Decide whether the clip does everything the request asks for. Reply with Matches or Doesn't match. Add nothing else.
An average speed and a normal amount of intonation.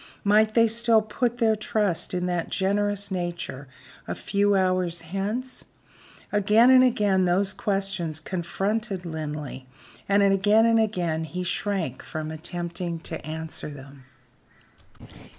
Doesn't match